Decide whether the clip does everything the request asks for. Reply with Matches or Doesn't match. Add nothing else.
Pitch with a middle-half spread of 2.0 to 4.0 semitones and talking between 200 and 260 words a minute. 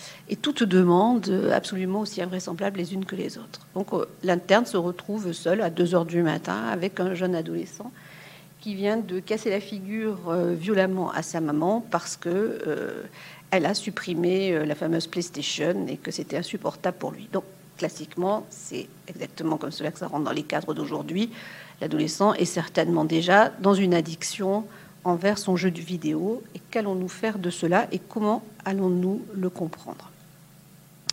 Doesn't match